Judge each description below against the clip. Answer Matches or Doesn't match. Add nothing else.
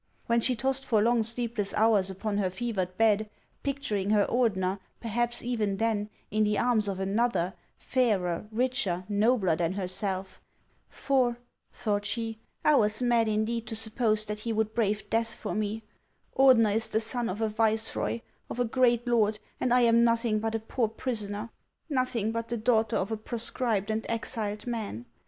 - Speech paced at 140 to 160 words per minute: Doesn't match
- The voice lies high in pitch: Matches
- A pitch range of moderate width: Doesn't match